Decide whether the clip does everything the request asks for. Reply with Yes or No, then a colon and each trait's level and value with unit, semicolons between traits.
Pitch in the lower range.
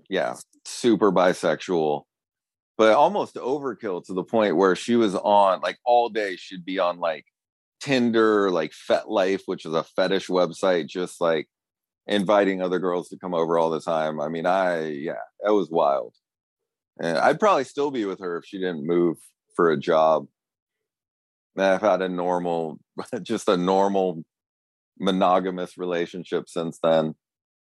Yes: very low, 90 Hz